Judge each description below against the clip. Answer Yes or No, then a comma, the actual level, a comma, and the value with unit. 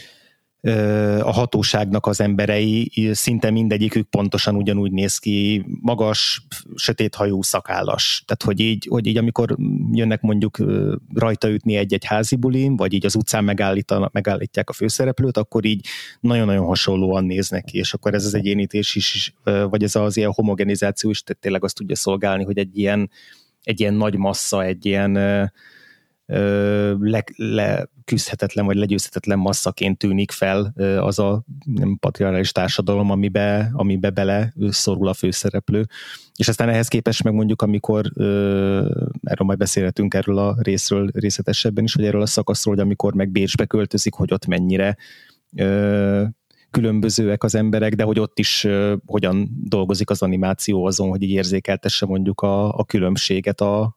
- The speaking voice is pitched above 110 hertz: No, low, 105 Hz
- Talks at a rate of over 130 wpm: Yes, average, 150 wpm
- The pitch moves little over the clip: Yes, narrow, 1.7 semitones